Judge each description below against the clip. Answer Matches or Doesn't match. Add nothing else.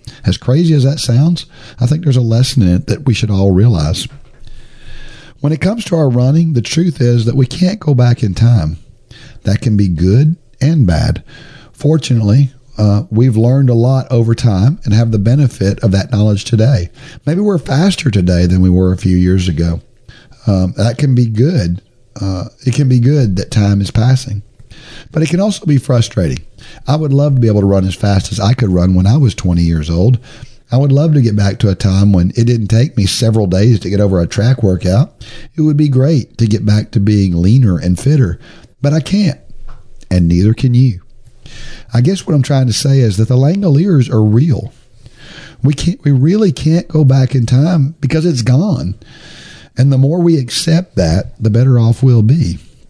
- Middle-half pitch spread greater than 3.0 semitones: Matches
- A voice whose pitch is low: Matches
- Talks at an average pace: Doesn't match